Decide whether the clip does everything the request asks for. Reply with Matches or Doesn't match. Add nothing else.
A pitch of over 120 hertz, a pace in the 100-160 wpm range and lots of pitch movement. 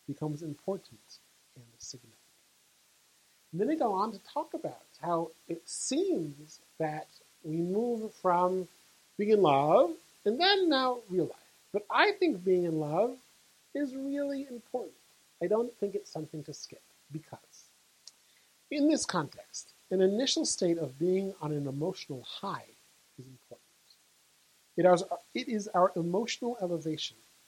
Matches